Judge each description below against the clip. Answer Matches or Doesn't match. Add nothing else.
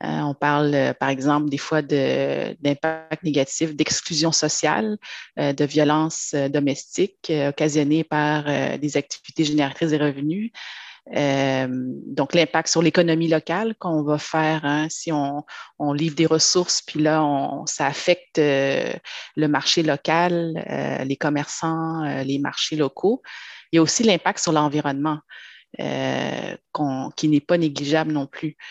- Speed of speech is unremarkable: Doesn't match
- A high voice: Doesn't match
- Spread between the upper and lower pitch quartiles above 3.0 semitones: Doesn't match